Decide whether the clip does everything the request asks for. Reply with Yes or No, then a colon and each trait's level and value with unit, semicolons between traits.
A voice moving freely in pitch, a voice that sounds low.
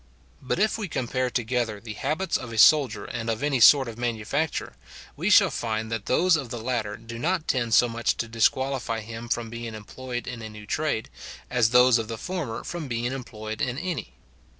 No: average, 2.9 semitones; low, 120 Hz